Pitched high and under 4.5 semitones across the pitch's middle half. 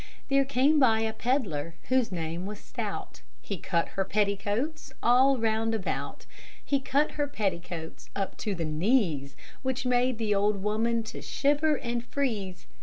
No: high, 225 Hz; average, 5.1 semitones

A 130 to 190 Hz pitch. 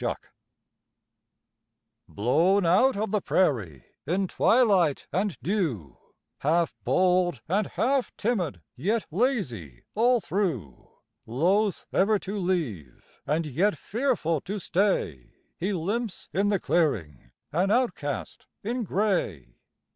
Yes: medium, 185 Hz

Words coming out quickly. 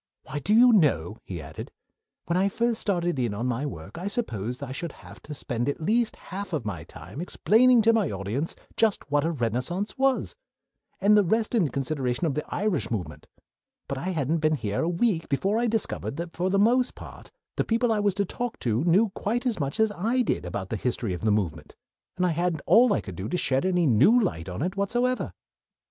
Yes: fast, 220 wpm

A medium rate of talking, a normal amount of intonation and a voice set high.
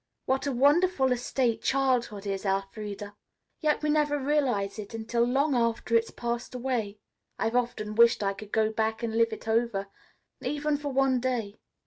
Yes: average, 170 wpm; average, 3.7 semitones; high, 235 Hz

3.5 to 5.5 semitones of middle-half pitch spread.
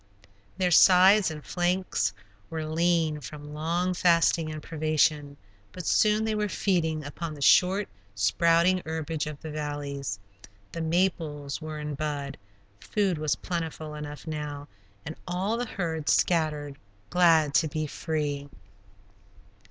No: average, 2.9 semitones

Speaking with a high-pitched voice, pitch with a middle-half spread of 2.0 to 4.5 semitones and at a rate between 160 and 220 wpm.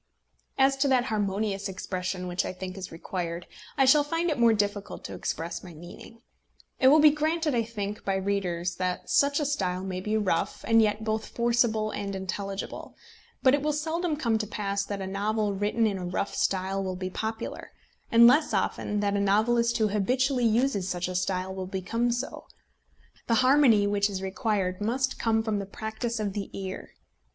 Yes: high, 210 Hz; average, 3.9 semitones; average, 190 wpm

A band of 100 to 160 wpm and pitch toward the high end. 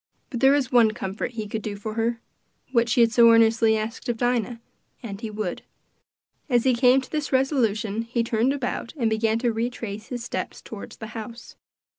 No: average, 195 wpm; high, 230 Hz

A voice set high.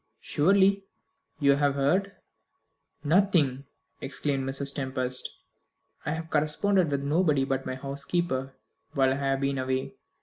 No: medium, 140 Hz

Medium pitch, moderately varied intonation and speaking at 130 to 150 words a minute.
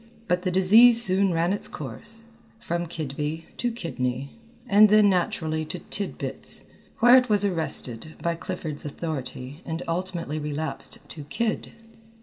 Yes: medium, 170 Hz; average, 4.9 semitones; slow, 135 wpm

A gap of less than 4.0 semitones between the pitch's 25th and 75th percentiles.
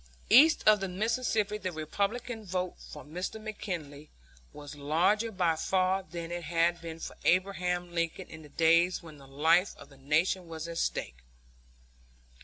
Yes: average, 3.4 semitones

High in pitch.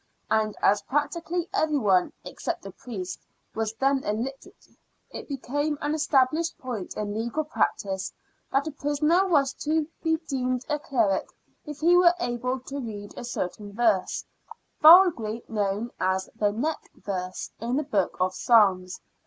Yes: very high, 255 Hz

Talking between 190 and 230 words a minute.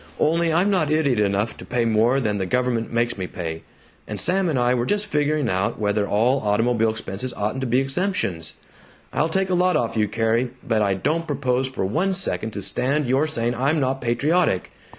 Yes: fast, 205 wpm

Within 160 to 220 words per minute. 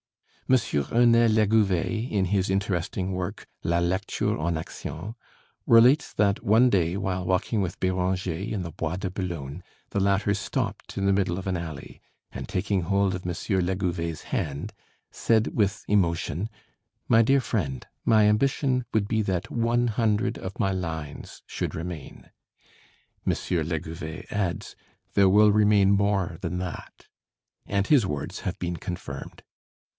No: average, 145 wpm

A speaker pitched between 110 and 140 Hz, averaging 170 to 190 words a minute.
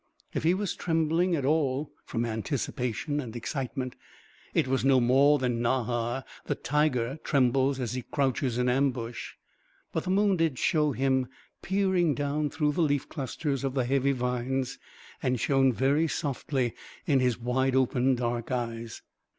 No: low, 135 Hz; average, 155 wpm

